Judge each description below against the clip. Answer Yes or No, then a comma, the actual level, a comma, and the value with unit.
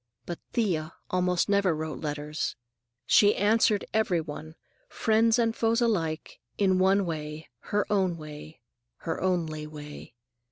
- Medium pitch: Yes, medium, 180 Hz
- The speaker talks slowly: Yes, slow, 130 wpm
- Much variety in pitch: No, average, 4.8 semitones